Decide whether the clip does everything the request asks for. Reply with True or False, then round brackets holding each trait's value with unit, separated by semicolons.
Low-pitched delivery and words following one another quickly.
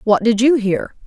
False (230 Hz; 225 wpm)